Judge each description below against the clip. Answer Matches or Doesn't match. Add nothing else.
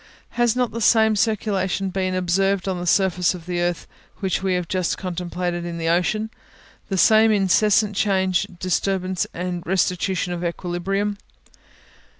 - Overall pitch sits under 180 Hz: Doesn't match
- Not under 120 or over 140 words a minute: Doesn't match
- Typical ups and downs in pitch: Doesn't match